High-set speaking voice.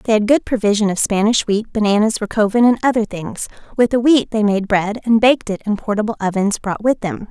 Yes: high, 215 Hz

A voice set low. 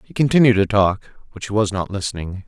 Yes: low, 105 Hz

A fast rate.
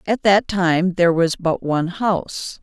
No: average, 185 wpm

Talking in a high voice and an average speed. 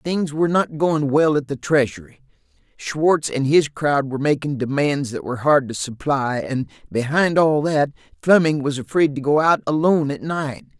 No: medium, 145 Hz; average, 185 wpm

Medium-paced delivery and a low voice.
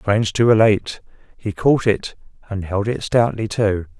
Yes: average, 165 wpm; low, 105 Hz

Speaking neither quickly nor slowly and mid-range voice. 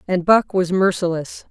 Yes: average, 160 wpm; medium, 180 Hz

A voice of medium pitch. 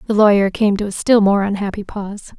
No: high, 205 Hz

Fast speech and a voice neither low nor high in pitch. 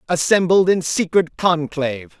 No: slow, 110 wpm; medium, 165 Hz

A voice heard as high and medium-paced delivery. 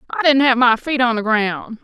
No: high, 235 Hz; fast, 260 wpm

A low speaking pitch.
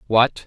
Yes: low, 120 Hz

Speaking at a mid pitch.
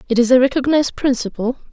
No: very high, 255 Hz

